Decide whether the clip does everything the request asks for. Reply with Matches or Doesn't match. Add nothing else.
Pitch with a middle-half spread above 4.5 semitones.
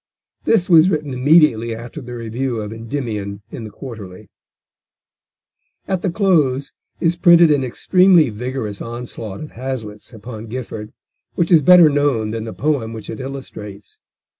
Matches